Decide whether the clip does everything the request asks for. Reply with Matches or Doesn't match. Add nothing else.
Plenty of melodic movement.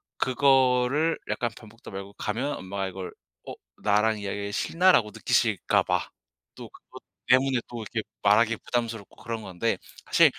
Doesn't match